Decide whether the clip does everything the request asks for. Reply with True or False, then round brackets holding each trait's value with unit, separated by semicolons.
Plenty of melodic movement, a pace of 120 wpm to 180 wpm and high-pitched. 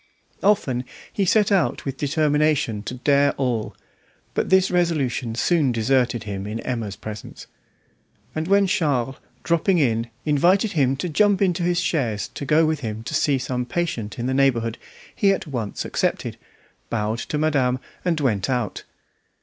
False (6.2 semitones; 160 wpm; 135 Hz)